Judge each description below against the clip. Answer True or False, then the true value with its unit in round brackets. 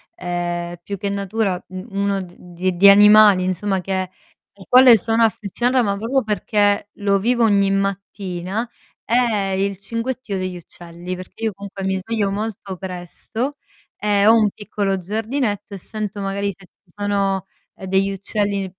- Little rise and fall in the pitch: True (2.2 semitones)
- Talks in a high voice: True (200 Hz)